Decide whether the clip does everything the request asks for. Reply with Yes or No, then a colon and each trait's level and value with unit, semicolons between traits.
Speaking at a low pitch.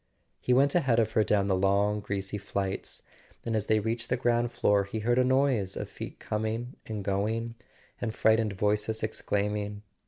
Yes: low, 110 Hz